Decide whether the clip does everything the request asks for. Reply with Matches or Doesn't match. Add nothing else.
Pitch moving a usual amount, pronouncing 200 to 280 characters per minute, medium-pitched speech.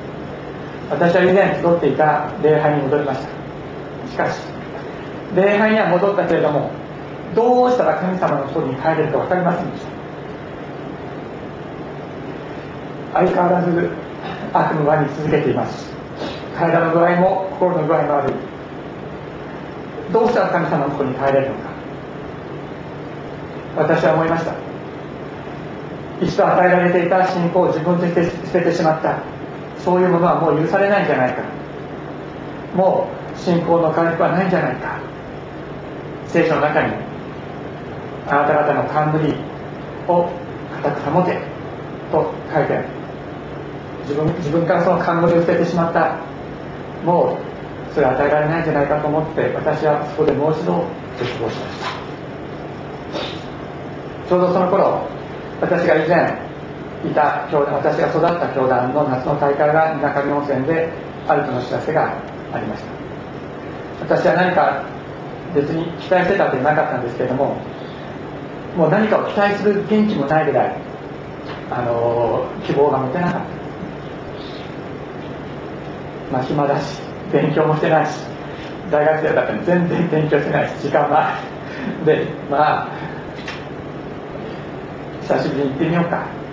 Matches